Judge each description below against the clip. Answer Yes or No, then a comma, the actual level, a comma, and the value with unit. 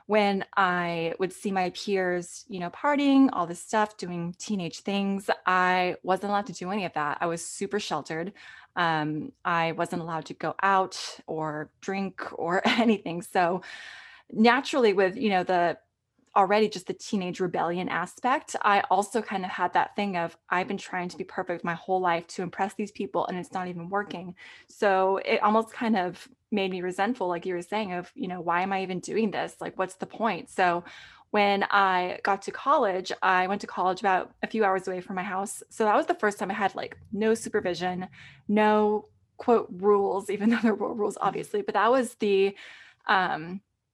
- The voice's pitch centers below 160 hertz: No, high, 190 Hz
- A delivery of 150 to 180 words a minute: No, average, 195 wpm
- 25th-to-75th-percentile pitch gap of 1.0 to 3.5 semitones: Yes, average, 3.0 semitones